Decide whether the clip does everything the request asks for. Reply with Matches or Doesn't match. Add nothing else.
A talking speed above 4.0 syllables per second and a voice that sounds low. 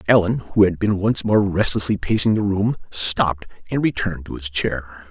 Matches